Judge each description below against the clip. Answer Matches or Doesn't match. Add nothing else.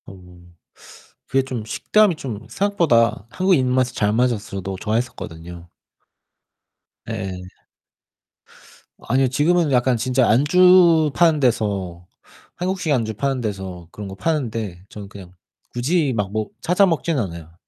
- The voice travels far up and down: Matches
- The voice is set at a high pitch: Doesn't match